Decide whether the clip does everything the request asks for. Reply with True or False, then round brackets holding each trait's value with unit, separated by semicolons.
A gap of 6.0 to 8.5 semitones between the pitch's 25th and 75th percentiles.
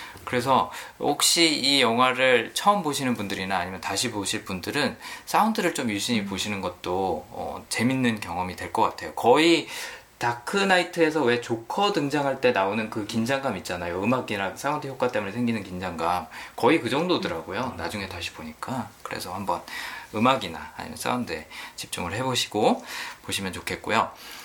True (6.4 semitones)